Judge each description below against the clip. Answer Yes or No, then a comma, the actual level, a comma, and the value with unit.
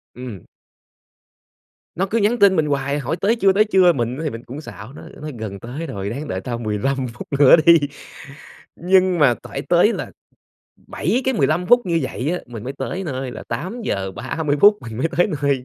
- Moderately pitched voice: Yes, medium, 145 Hz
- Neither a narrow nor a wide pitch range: No, wide, 6.5 semitones